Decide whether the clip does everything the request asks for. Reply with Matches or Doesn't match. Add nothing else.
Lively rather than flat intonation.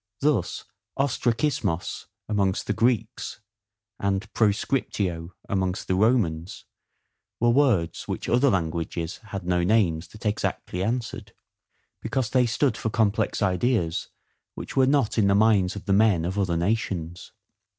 Doesn't match